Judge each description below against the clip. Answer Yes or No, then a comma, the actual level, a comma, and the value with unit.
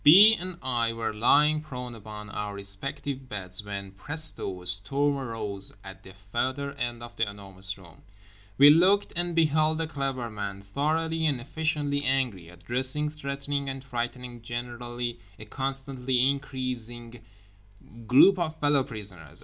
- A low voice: Yes, low, 125 Hz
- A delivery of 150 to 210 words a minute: No, average, 140 wpm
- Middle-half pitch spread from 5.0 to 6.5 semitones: Yes, average, 5.3 semitones